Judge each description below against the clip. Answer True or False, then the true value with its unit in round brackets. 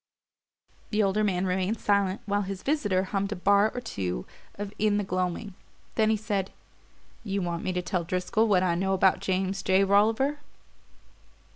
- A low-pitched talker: False (195 Hz)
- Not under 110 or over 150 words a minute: False (170 wpm)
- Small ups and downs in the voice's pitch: True (2.0 semitones)